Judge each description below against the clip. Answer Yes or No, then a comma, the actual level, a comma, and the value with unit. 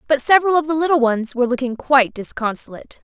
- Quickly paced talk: No, average, 195 wpm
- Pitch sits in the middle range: No, very high, 270 Hz